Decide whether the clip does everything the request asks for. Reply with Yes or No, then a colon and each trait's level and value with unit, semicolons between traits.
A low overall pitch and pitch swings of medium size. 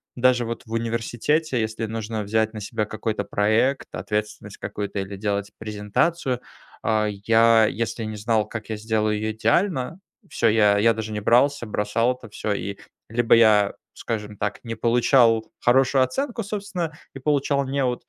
Yes: low, 115 Hz; average, 3.0 semitones